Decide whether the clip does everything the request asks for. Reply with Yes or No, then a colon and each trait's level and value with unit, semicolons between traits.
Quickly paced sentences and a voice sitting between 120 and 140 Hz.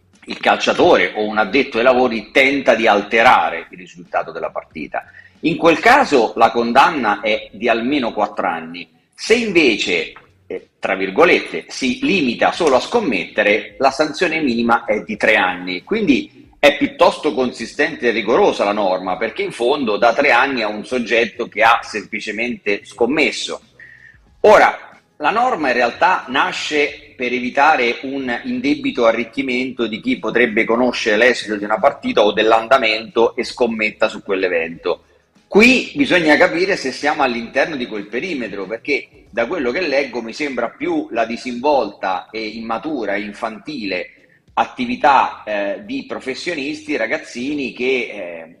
No: average, 145 wpm; low, 135 Hz